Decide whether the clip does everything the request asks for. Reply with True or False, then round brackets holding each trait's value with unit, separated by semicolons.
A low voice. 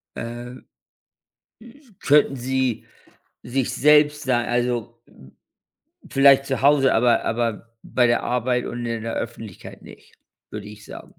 True (120 Hz)